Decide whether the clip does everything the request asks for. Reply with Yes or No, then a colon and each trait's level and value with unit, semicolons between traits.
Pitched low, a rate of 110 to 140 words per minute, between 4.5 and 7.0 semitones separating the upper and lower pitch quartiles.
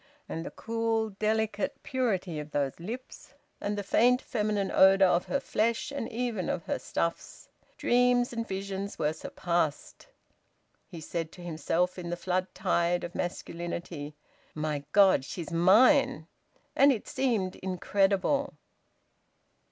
No: high, 190 Hz; slow, 135 wpm; average, 4.8 semitones